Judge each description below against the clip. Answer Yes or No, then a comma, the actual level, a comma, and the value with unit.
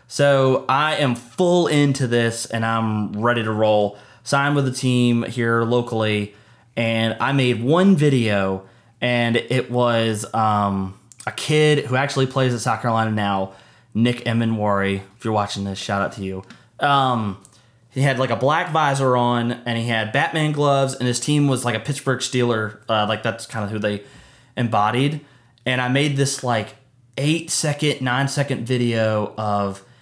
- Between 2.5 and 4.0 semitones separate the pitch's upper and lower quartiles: Yes, average, 3.4 semitones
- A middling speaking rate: Yes, average, 170 wpm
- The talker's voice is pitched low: Yes, low, 120 Hz